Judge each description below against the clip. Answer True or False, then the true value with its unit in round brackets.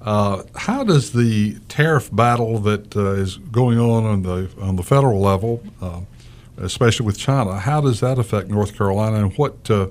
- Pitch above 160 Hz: False (110 Hz)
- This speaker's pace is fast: False (180 wpm)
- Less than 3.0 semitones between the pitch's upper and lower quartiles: False (3.5 semitones)